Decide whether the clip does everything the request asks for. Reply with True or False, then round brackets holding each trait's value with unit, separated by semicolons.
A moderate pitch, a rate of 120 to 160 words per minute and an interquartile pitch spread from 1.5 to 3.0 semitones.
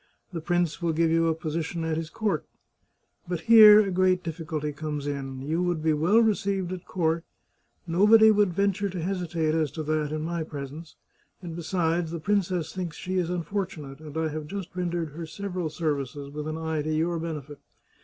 False (165 Hz; 195 wpm; 2.7 semitones)